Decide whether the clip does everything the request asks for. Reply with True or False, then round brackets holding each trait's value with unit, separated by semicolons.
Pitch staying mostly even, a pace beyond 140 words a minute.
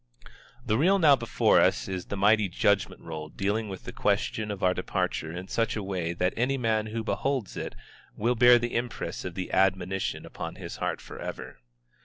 False (4.0 semitones; 190 wpm)